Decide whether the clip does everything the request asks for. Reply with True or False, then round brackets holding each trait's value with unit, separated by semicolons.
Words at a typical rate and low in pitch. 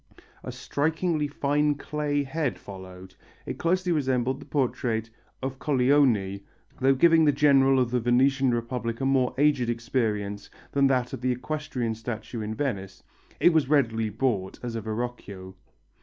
True (150 wpm; 130 Hz)